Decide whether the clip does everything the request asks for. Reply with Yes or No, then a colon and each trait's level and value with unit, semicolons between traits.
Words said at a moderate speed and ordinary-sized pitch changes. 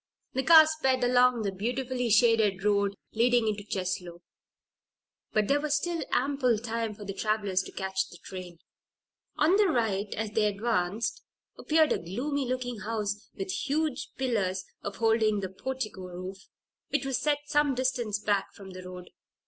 Yes: average, 160 wpm; average, 4.9 semitones